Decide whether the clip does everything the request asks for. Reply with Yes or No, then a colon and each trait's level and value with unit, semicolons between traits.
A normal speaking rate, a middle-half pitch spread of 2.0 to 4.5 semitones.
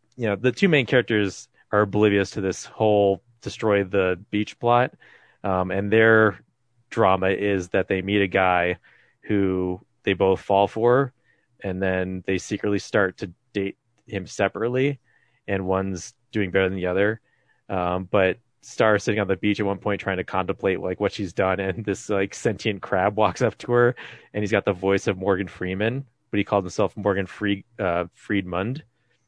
Yes: average, 180 wpm; narrow, 2.5 semitones